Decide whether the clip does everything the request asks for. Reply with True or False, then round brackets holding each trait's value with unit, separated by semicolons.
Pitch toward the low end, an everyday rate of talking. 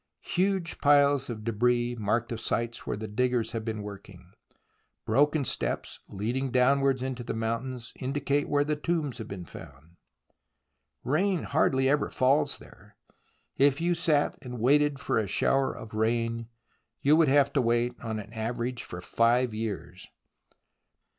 True (125 Hz; 150 wpm)